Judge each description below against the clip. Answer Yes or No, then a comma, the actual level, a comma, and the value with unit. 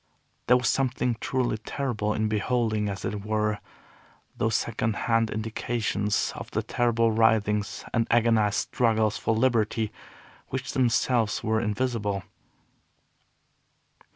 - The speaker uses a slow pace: Yes, slow, 115 wpm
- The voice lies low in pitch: Yes, low, 110 Hz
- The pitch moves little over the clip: Yes, narrow, 2.0 semitones